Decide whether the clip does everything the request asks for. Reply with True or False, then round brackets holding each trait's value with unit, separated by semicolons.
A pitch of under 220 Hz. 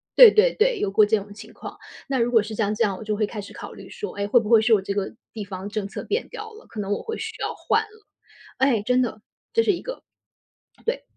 False (225 Hz)